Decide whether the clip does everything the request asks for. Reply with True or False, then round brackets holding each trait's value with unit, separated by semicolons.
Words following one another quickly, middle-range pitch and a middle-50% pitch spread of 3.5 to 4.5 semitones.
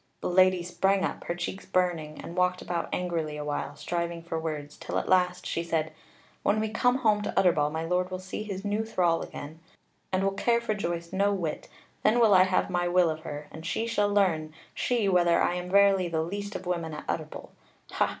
False (220 wpm; 180 Hz; 3.0 semitones)